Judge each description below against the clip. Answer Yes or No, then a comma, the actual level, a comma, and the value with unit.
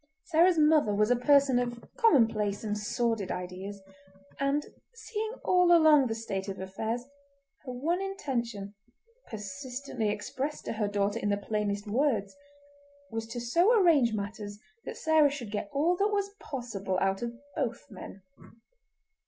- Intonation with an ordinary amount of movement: No, wide, 6.4 semitones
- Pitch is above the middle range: Yes, high, 235 Hz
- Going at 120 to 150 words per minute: Yes, average, 145 wpm